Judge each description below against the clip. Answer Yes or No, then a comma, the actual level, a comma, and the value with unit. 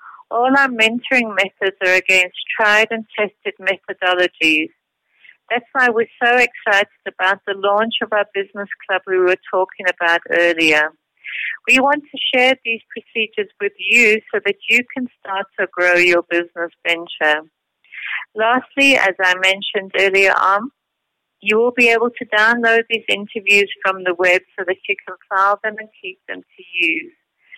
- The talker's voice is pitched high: Yes, high, 200 Hz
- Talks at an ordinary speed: Yes, average, 160 wpm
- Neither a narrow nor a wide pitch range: Yes, average, 3.8 semitones